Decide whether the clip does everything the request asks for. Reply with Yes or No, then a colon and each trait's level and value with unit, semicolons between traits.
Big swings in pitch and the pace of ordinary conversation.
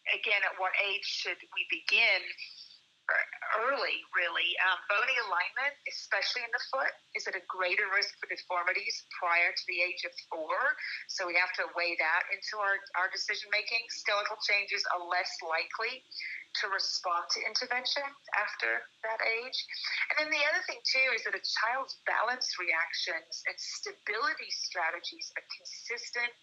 Yes: wide, 6.2 semitones; average, 155 wpm